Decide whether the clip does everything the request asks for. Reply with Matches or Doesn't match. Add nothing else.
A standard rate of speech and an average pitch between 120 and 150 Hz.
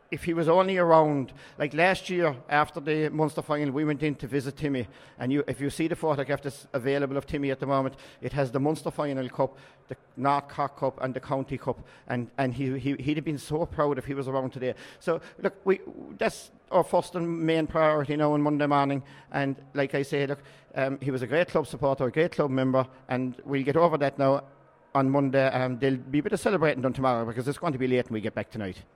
Doesn't match